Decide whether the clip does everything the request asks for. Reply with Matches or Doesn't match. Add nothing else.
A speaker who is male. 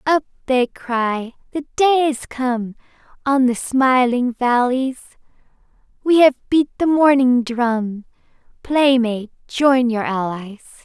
Doesn't match